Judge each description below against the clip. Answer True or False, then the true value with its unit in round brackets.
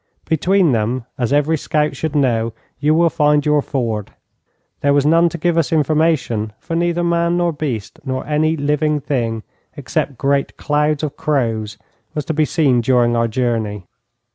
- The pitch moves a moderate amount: True (4.6 semitones)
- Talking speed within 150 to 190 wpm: True (165 wpm)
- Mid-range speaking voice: True (145 Hz)